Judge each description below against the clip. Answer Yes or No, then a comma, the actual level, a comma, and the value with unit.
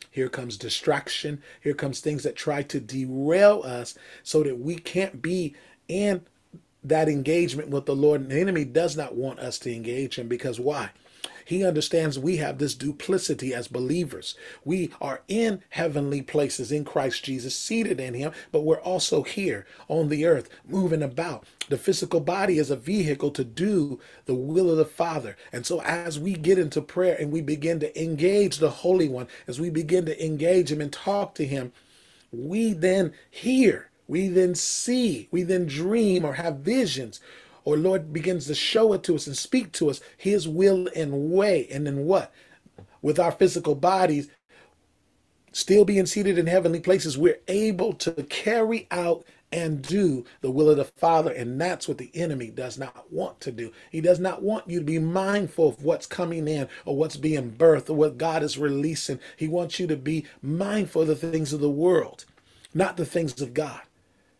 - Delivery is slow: No, average, 185 wpm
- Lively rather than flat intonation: No, average, 4.1 semitones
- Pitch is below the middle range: No, medium, 160 Hz